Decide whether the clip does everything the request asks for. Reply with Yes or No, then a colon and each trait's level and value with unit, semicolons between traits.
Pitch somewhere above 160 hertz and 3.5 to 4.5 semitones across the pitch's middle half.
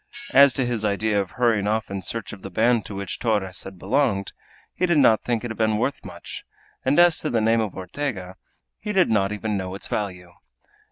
No: low, 110 Hz; average, 3.8 semitones